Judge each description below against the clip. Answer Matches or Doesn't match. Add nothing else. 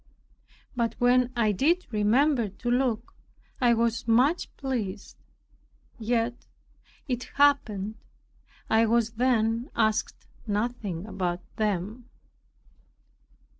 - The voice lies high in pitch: Matches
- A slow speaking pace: Matches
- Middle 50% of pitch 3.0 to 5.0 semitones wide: Doesn't match